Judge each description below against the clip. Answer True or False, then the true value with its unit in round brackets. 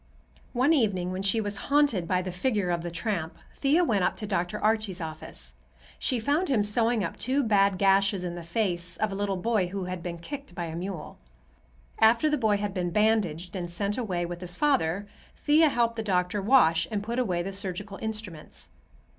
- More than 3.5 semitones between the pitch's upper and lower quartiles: True (4.1 semitones)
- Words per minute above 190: True (200 wpm)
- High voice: True (200 Hz)